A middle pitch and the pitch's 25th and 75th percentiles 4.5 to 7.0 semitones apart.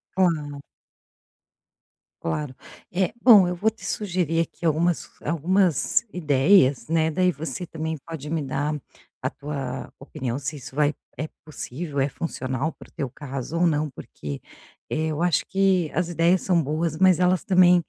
No: medium, 160 Hz; average, 3.6 semitones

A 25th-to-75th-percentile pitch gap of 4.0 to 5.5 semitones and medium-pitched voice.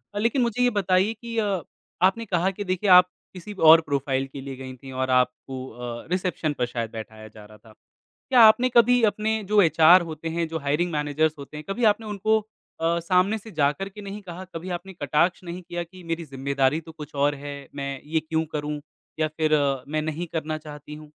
Yes: average, 4.9 semitones; medium, 165 Hz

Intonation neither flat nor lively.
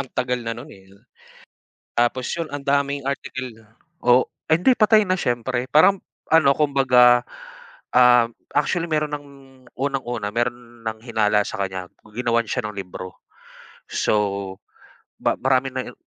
Yes: average, 3.4 semitones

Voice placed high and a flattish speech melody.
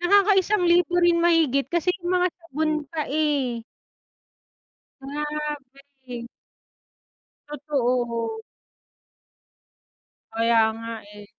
No: very high, 295 Hz; wide, 5.5 semitones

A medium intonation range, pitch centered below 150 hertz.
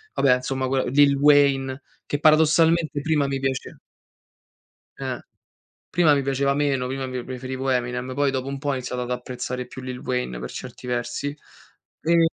No: narrow, 2.1 semitones; low, 135 Hz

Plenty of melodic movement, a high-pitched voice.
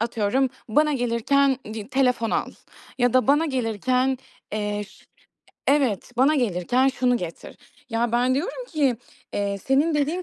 No: average, 3.5 semitones; very high, 255 Hz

